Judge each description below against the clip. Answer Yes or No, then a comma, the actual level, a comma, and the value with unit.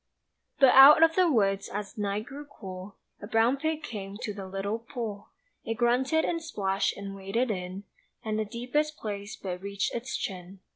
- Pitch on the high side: Yes, high, 215 Hz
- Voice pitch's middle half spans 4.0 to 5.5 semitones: Yes, average, 4.8 semitones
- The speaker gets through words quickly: No, average, 180 wpm